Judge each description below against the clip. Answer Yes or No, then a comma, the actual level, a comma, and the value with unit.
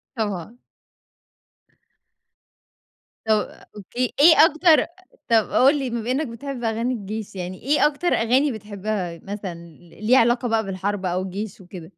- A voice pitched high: Yes, high, 220 Hz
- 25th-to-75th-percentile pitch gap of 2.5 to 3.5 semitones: No, average, 4.8 semitones